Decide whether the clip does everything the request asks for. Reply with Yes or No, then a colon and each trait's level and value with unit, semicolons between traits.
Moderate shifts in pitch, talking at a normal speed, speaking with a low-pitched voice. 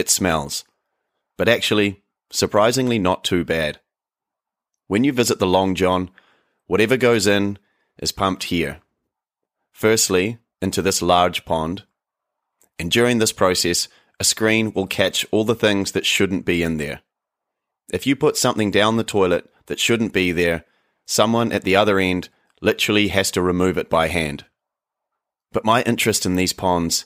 Yes: average, 3.7 semitones; average, 155 wpm; very low, 95 Hz